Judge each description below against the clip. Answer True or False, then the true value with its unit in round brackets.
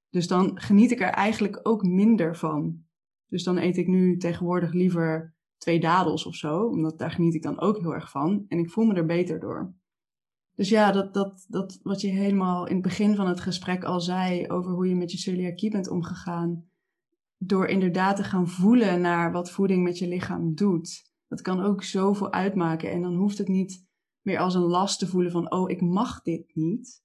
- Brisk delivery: True (210 wpm)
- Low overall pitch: False (180 Hz)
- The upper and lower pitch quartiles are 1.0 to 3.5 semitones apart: True (2.4 semitones)